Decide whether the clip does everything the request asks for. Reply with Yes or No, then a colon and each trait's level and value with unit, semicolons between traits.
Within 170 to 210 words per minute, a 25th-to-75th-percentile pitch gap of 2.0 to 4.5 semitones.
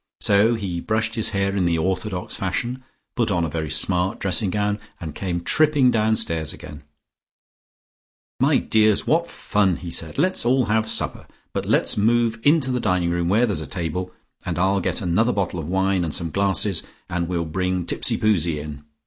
Yes: average, 180 wpm; average, 4.2 semitones